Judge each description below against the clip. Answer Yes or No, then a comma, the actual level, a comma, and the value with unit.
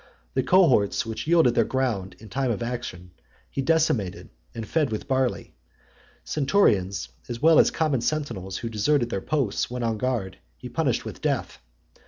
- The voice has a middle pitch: No, low, 120 Hz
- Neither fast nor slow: Yes, average, 165 wpm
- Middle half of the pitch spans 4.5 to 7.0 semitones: Yes, average, 5.2 semitones